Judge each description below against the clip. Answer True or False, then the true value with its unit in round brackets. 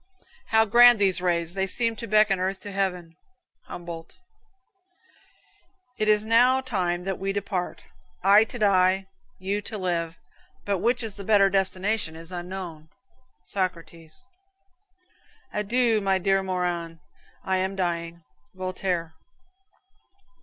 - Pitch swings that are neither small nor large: True (3.0 semitones)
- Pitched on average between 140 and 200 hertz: True (190 Hz)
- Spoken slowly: True (125 wpm)